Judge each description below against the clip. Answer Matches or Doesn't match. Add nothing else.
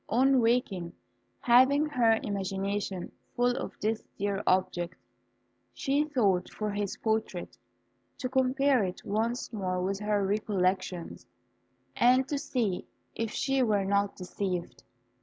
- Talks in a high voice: Matches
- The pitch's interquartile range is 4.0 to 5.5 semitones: Matches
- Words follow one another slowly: Matches